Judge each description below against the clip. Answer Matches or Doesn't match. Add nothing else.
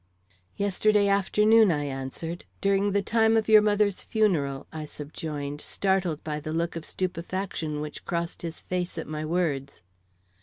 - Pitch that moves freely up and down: Doesn't match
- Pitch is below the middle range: Doesn't match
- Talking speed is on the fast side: Doesn't match